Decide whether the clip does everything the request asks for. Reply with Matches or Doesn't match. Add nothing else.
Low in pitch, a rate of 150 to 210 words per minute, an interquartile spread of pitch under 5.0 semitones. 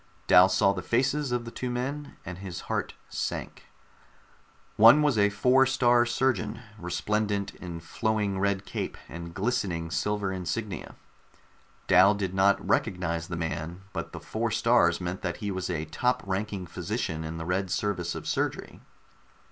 Matches